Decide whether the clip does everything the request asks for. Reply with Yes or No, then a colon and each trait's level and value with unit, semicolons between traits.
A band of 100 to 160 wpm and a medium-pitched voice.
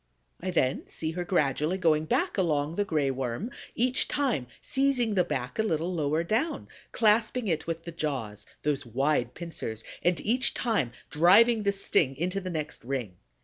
No: average, 170 wpm; medium, 165 Hz